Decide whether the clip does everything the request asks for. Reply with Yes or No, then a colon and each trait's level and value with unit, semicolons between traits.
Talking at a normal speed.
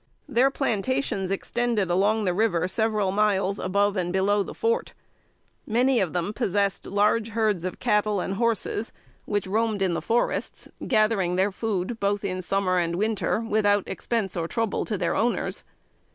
Yes: average, 160 wpm